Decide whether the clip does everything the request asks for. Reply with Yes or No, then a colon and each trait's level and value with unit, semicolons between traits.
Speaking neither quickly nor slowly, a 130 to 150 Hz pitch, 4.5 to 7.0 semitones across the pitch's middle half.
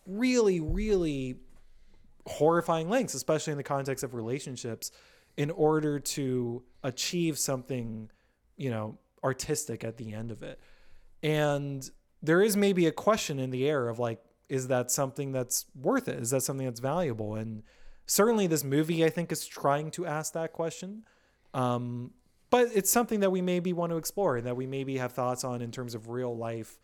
Yes: average, 175 wpm; medium, 140 Hz; average, 5.0 semitones